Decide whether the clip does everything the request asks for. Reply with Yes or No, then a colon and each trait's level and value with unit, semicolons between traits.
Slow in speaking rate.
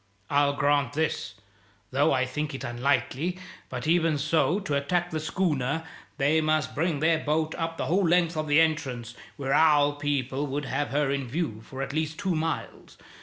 No: average, 180 wpm